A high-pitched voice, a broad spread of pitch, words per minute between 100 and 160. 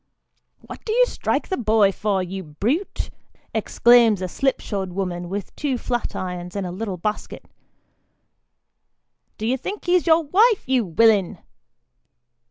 Yes: high, 215 Hz; wide, 6.2 semitones; average, 150 wpm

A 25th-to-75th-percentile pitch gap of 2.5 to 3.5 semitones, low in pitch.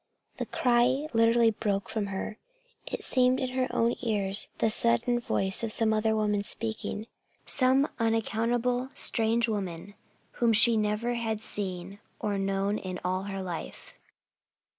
No: average, 2.8 semitones; high, 220 Hz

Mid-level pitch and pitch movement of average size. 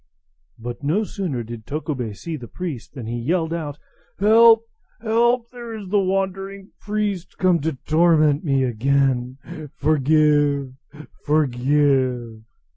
No: medium, 155 Hz; wide, 6.6 semitones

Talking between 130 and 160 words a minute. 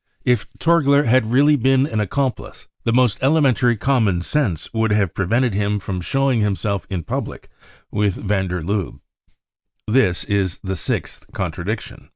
Yes: average, 150 wpm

